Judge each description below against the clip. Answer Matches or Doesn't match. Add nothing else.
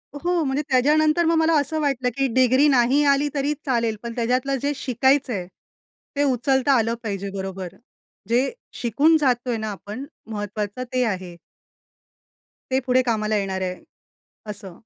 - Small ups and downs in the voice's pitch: Doesn't match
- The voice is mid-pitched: Doesn't match